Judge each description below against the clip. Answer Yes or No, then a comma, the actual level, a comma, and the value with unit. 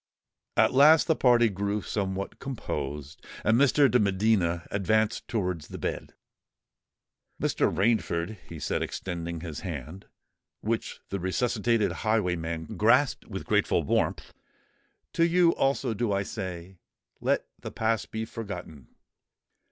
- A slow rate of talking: Yes, slow, 125 wpm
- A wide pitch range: No, average, 4.8 semitones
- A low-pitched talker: Yes, low, 100 Hz